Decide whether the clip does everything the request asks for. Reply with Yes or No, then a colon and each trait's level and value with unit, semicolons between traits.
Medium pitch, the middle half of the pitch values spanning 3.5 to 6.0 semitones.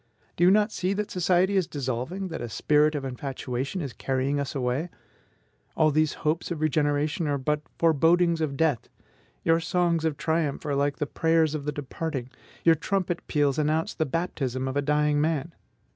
No: medium, 155 Hz; average, 2.8 semitones